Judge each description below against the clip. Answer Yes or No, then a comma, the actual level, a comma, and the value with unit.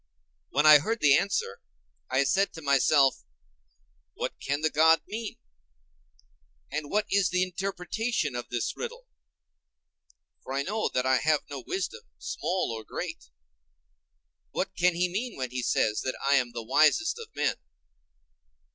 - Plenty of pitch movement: Yes, wide, 6.7 semitones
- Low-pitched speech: No, medium, 155 Hz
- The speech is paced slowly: No, average, 150 wpm